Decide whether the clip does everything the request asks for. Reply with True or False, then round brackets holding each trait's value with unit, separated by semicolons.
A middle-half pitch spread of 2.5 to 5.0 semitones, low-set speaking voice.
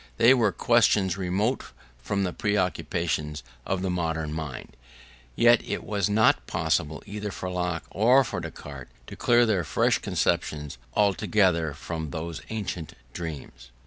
True (4.6 semitones; 90 Hz)